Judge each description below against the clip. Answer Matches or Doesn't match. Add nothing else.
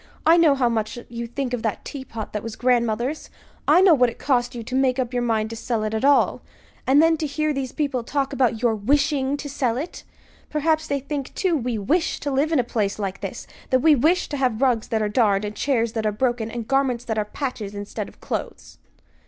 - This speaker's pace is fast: Matches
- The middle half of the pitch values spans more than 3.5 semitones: Matches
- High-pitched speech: Matches